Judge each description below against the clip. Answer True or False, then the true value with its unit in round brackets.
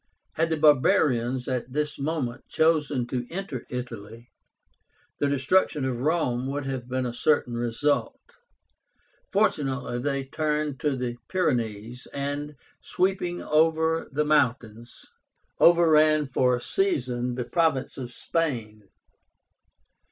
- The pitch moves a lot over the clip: False (3.9 semitones)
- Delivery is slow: True (115 wpm)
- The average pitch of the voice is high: False (135 Hz)